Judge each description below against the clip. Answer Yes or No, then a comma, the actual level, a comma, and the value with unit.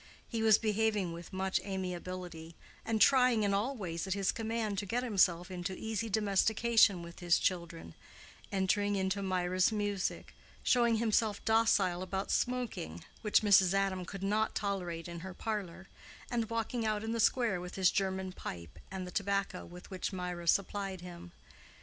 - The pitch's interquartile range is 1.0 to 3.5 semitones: Yes, average, 3.2 semitones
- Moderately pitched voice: No, high, 195 Hz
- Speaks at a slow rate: No, average, 160 wpm